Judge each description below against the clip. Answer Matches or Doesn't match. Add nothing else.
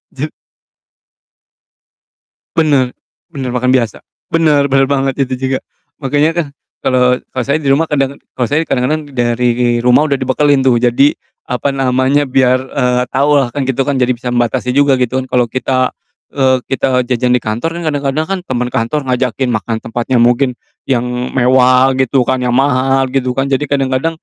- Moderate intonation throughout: Doesn't match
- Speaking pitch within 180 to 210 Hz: Doesn't match